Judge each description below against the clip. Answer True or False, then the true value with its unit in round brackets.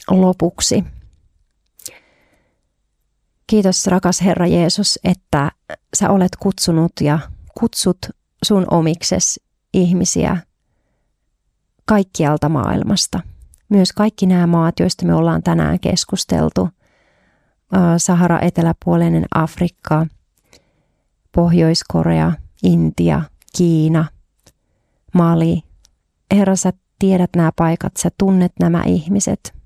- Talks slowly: True (85 wpm)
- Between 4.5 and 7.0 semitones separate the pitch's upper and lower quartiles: False (3.6 semitones)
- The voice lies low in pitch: False (170 Hz)